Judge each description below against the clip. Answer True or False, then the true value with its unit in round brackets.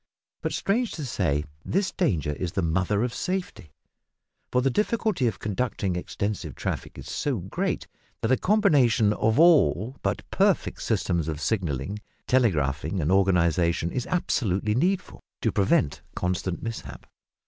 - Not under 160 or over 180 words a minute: False (140 wpm)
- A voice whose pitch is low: True (105 Hz)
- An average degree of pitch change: False (7.3 semitones)